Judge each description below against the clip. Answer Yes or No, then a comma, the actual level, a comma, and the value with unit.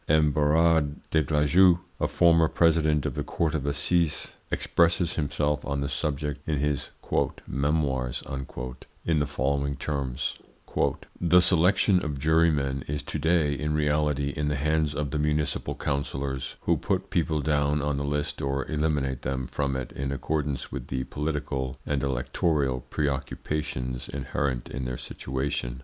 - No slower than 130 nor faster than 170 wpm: Yes, average, 150 wpm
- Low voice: Yes, very low, 75 Hz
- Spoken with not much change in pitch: Yes, narrow, 2.2 semitones